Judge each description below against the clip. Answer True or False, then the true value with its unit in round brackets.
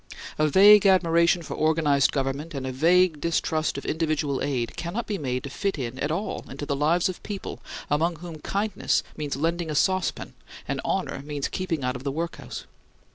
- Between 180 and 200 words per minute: True (185 wpm)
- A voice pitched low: False (155 Hz)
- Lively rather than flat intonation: False (3.8 semitones)